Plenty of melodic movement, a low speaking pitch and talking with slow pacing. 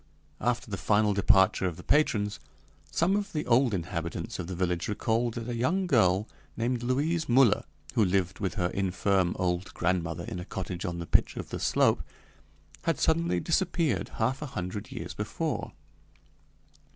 No: wide, 5.9 semitones; low, 105 Hz; average, 165 wpm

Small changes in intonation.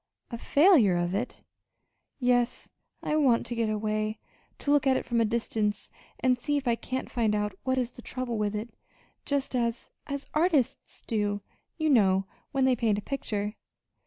No: average, 3.7 semitones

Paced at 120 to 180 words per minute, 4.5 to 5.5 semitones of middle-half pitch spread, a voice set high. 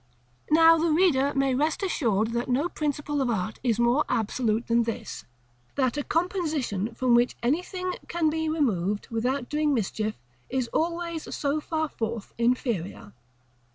Yes: average, 150 wpm; average, 5.2 semitones; very high, 265 Hz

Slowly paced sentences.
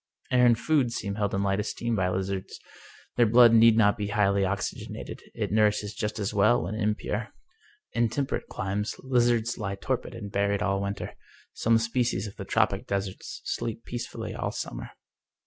No: average, 180 wpm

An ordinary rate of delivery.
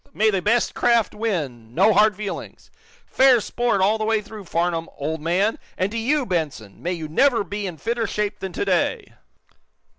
Yes: average, 180 wpm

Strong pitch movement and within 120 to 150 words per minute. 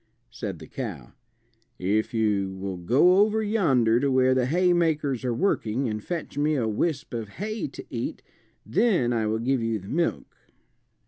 No: wide, 7.2 semitones; average, 170 wpm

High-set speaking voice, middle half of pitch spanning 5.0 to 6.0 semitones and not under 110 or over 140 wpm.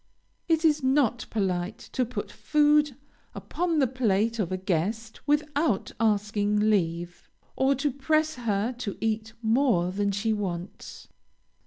Yes: high, 225 Hz; wide, 5.6 semitones; slow, 135 wpm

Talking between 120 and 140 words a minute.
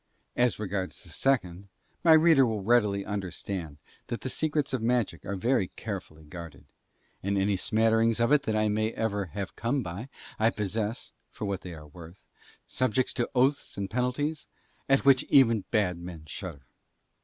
No: average, 165 wpm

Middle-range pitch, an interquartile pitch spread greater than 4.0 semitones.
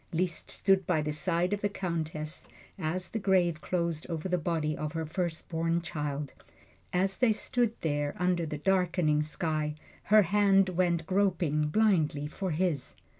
No: medium, 170 Hz; average, 3.5 semitones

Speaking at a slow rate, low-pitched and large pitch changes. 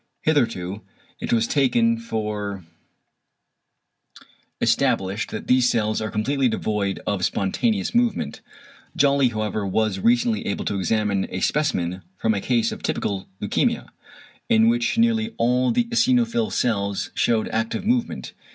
Yes: slow, 130 wpm; low, 115 Hz; wide, 6.4 semitones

